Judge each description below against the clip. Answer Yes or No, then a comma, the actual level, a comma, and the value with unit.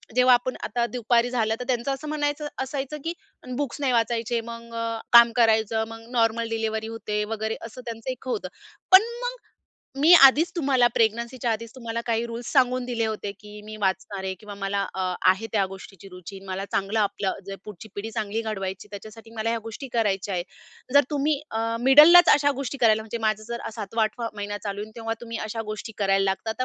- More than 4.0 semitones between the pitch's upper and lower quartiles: No, average, 2.8 semitones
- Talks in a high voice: Yes, high, 225 Hz